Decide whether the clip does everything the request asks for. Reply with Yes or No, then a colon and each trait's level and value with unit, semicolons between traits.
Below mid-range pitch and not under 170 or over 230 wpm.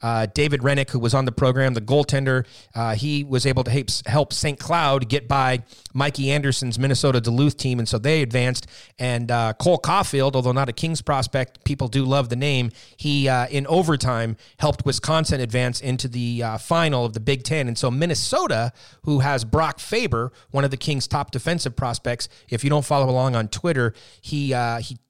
Yes: low, 130 Hz; average, 200 wpm